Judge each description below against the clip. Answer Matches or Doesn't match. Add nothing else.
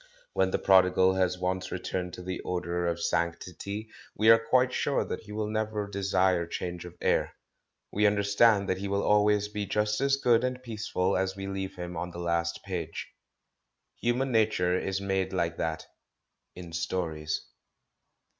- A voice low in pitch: Matches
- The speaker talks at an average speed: Matches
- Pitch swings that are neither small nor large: Matches